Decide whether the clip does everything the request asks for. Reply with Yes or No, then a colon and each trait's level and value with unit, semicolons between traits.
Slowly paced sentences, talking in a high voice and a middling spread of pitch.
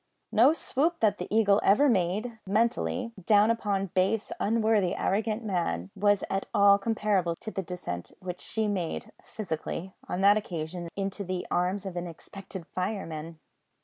No: average, 150 wpm; high, 195 Hz; average, 3.3 semitones